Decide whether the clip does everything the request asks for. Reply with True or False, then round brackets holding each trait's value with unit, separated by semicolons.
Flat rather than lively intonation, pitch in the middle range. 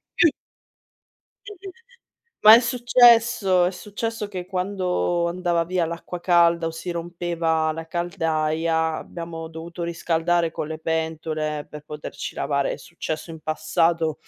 True (1.9 semitones; 170 Hz)